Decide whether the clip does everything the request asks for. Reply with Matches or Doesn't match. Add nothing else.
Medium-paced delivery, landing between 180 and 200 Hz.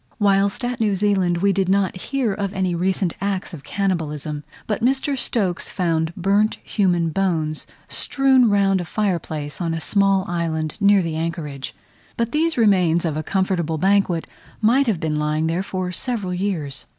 Matches